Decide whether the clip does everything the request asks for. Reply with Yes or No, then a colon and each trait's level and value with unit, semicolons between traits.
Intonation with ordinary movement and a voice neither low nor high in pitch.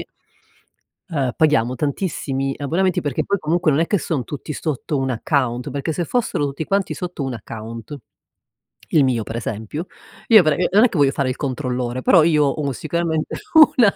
Yes: average, 4.5 semitones; medium, 145 Hz